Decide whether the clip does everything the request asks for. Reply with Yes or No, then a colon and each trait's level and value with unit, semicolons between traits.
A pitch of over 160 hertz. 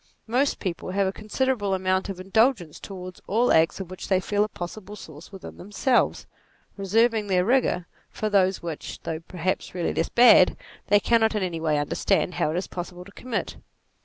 Yes: high, 190 Hz